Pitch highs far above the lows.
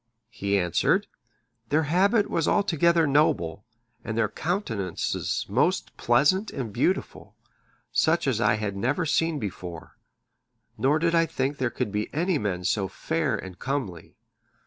Yes: wide, 8.1 semitones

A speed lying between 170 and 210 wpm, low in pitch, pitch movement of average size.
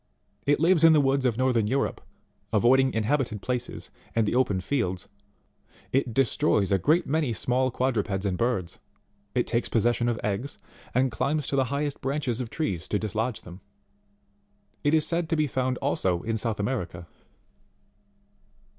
No: average, 160 wpm; low, 125 Hz; average, 4.3 semitones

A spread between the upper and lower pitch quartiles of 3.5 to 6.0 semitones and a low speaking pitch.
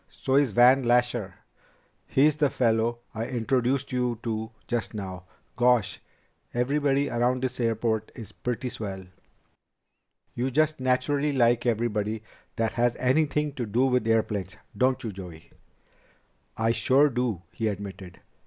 No: average, 2.8 semitones; low, 120 Hz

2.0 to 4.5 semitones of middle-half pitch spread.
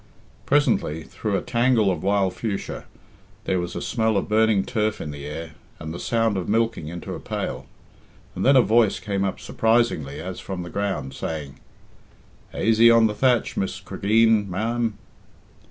Yes: average, 4.2 semitones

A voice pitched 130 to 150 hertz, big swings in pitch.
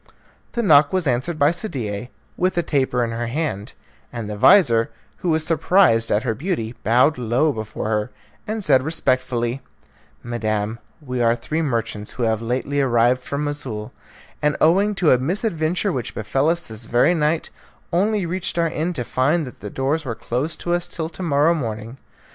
Yes: low, 135 Hz; wide, 6.0 semitones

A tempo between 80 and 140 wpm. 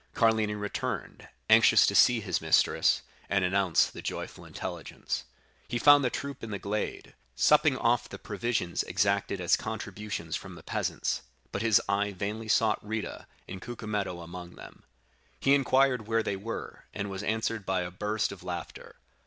No: average, 160 wpm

